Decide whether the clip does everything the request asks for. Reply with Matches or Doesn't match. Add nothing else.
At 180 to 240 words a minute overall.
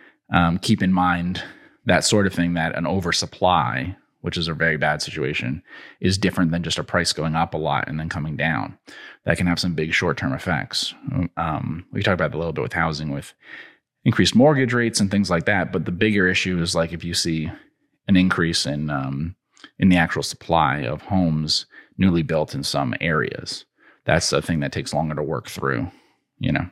Matches